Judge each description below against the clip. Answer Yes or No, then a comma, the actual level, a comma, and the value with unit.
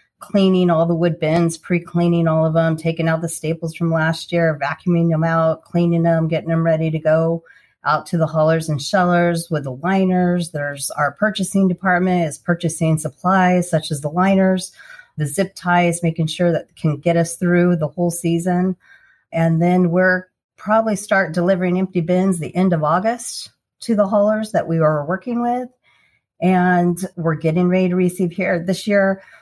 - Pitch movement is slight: Yes, narrow, 2.2 semitones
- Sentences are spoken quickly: No, average, 180 wpm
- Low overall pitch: No, medium, 175 Hz